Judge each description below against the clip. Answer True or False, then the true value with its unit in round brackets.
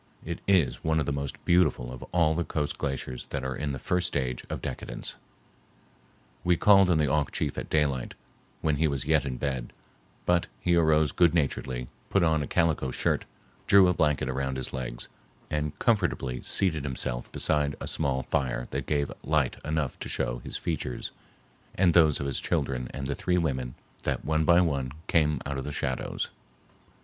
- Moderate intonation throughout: True (3.5 semitones)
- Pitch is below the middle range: True (75 Hz)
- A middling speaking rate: True (185 wpm)